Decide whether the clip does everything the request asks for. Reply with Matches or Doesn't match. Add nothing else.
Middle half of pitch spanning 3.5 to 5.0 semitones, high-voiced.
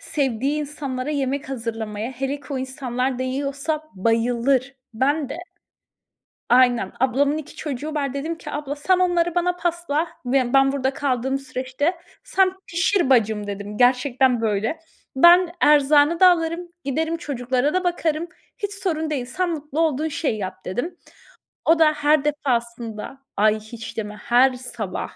Matches